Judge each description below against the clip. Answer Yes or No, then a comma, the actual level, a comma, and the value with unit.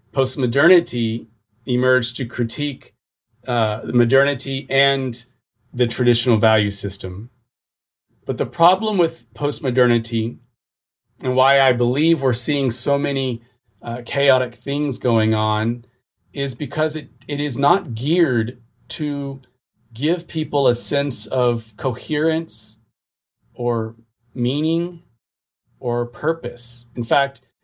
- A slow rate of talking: Yes, slow, 110 wpm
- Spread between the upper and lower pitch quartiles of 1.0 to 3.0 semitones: No, average, 3.4 semitones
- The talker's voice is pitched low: Yes, low, 125 Hz